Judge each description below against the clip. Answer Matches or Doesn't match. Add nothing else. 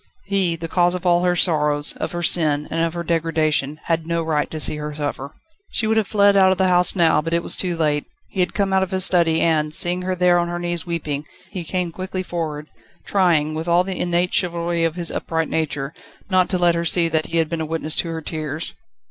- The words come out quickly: Matches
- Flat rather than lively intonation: Matches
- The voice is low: Doesn't match